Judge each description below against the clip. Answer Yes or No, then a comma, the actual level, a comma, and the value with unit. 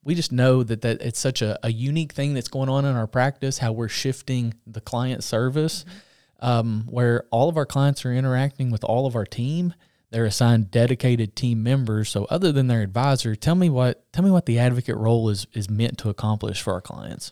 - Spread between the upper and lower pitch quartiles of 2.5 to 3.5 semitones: Yes, average, 3.0 semitones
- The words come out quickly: Yes, fast, 220 wpm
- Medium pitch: No, low, 125 Hz